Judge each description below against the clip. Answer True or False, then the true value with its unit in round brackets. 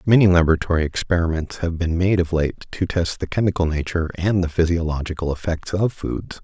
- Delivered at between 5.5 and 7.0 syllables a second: True (5.8 syllables/s)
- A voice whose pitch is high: False (85 Hz)